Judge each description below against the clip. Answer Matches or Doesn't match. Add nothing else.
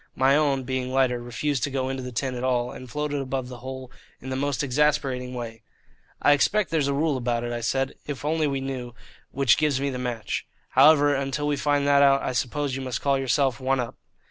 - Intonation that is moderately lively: Doesn't match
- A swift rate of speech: Matches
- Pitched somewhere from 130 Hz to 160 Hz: Matches